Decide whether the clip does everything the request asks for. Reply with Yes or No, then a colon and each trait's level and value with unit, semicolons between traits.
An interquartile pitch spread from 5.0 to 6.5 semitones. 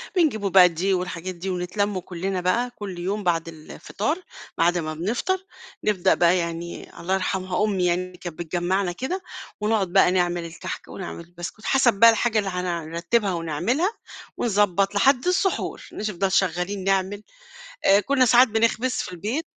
No: average, 3.7 semitones